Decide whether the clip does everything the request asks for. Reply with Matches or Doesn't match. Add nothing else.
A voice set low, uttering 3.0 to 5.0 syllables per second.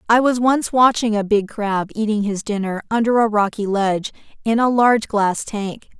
Doesn't match